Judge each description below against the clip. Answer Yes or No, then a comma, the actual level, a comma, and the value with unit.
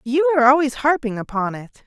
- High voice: Yes, very high, 255 Hz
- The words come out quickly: No, average, 195 wpm